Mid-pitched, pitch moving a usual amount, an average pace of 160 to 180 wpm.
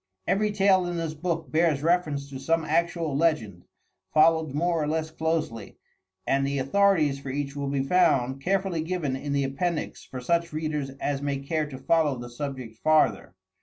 Yes: medium, 155 Hz; average, 3.4 semitones; average, 175 wpm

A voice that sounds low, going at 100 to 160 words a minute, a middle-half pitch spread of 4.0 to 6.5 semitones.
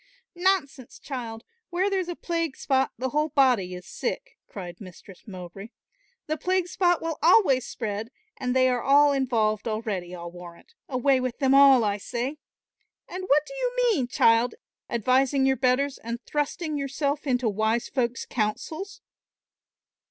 No: very high, 260 Hz; average, 150 wpm; average, 5.1 semitones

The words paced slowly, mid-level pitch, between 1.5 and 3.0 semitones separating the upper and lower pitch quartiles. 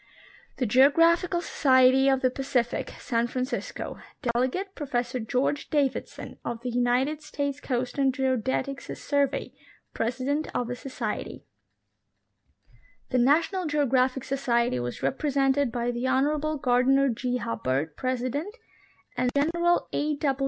No: slow, 115 wpm; very high, 265 Hz; narrow, 2.6 semitones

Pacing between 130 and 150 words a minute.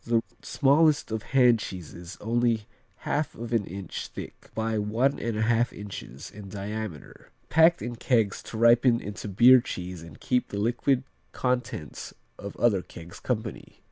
Yes: average, 145 wpm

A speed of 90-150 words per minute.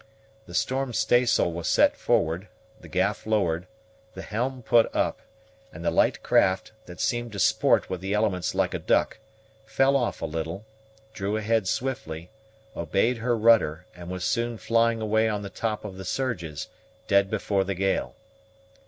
No: average, 165 wpm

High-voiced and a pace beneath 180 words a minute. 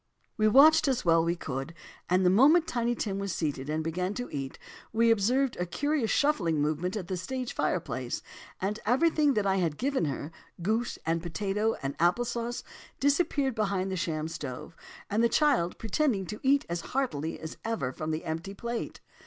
No: high, 200 Hz; average, 185 wpm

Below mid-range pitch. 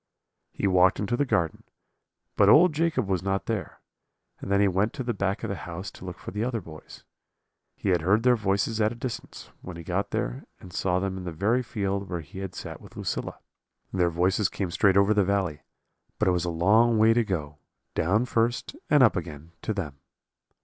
Yes: low, 100 Hz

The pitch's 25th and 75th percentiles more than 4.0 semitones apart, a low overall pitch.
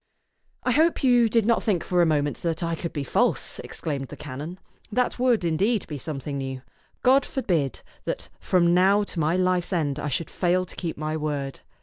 No: average, 5.1 semitones; medium, 170 Hz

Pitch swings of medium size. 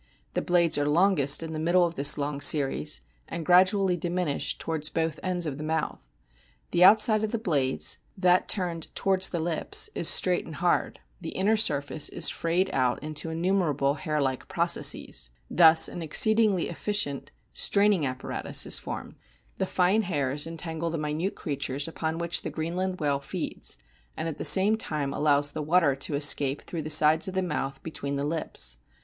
Yes: average, 3.8 semitones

